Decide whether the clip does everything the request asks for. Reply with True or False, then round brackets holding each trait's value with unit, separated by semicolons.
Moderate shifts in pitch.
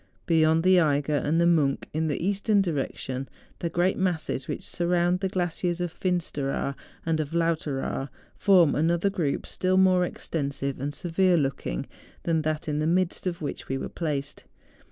True (3.5 semitones)